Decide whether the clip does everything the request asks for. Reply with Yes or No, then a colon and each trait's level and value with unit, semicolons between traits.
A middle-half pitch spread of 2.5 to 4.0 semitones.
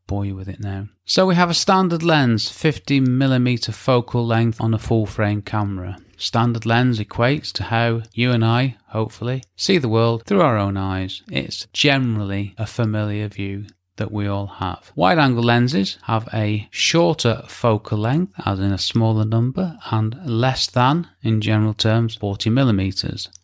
Yes: average, 3.5 semitones